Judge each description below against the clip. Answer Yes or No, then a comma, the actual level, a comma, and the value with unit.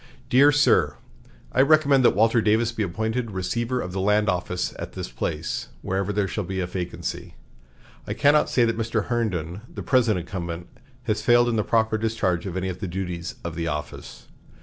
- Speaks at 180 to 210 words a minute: Yes, average, 190 wpm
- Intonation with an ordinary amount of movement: Yes, average, 4.5 semitones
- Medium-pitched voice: No, low, 105 Hz